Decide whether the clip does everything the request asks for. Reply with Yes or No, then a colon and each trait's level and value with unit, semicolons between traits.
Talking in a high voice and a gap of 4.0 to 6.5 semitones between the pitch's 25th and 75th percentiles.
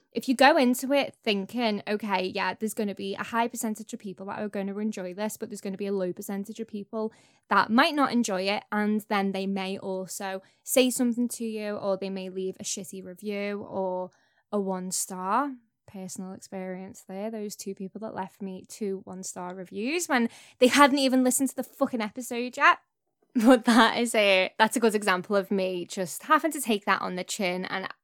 No: high, 205 Hz; average, 3.6 semitones